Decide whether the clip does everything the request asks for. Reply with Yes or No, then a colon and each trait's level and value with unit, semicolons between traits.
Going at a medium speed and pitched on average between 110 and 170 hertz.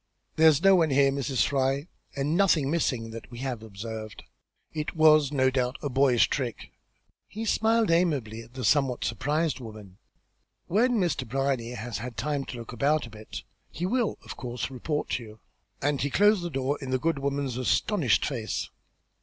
Yes: average, 180 wpm; low, 135 Hz